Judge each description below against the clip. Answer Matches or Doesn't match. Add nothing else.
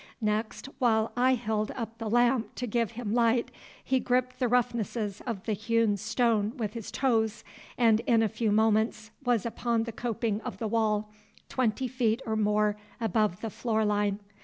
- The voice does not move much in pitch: Matches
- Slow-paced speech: Doesn't match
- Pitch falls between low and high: Doesn't match